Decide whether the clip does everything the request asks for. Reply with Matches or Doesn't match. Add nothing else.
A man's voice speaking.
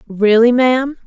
Doesn't match